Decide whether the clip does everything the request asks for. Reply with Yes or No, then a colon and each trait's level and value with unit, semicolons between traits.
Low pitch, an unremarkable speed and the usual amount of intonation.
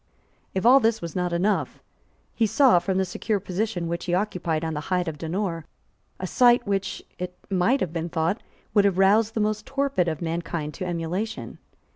No: medium, 185 Hz; average, 190 wpm; average, 4.0 semitones